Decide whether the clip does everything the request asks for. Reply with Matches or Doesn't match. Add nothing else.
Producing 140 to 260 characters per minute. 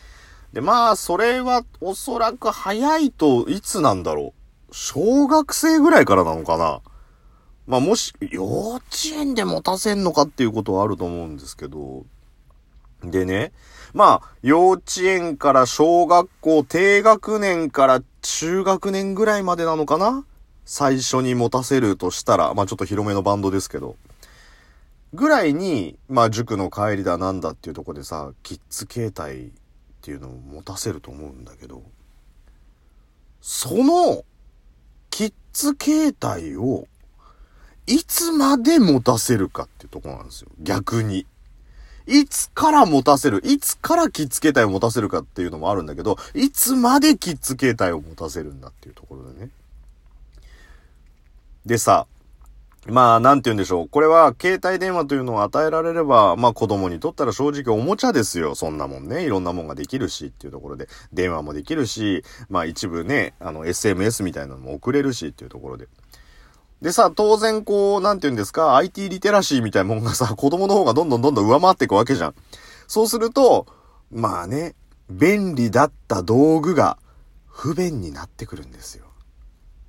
Doesn't match